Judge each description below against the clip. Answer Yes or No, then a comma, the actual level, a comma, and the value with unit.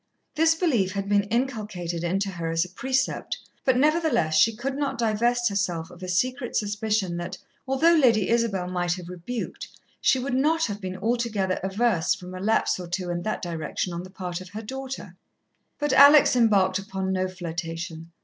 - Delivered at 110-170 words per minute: No, average, 180 wpm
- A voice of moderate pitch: No, high, 200 Hz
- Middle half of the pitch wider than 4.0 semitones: Yes, average, 5.3 semitones